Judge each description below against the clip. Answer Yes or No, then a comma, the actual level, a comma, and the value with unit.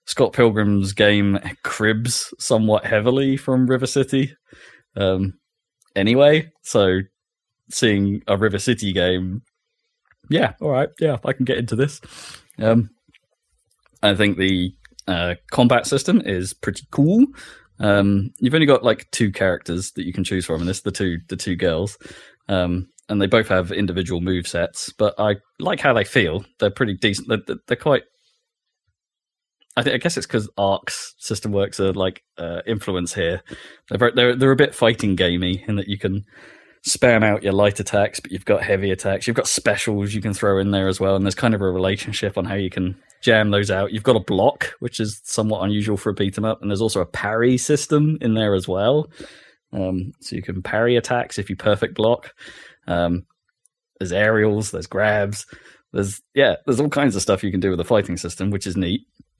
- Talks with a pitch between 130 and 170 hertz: No, low, 105 Hz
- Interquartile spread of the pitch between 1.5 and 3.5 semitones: No, average, 3.9 semitones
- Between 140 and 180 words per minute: No, average, 190 wpm